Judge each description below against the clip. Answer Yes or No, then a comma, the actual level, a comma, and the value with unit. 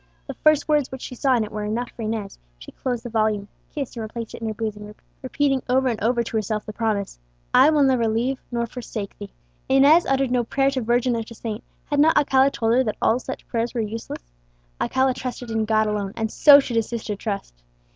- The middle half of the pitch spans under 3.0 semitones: No, average, 3.3 semitones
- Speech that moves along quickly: Yes, fast, 230 wpm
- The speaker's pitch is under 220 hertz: No, high, 235 Hz